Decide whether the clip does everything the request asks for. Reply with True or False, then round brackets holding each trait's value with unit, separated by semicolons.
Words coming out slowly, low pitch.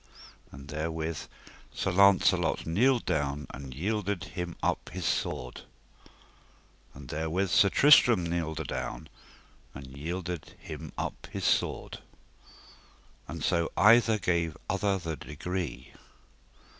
True (110 wpm; 85 Hz)